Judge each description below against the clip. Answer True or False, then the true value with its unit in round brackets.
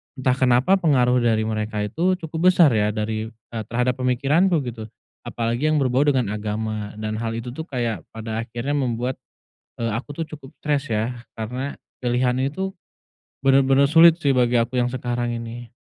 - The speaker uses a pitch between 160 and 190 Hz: False (125 Hz)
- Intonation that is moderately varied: True (3.5 semitones)